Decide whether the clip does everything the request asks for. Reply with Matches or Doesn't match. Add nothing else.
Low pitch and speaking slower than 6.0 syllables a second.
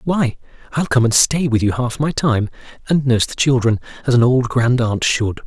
Matches